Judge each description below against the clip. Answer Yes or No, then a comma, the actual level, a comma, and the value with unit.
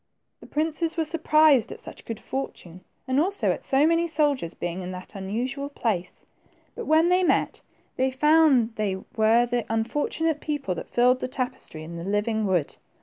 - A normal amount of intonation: No, wide, 6.8 semitones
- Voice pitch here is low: No, very high, 255 Hz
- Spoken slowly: No, average, 175 wpm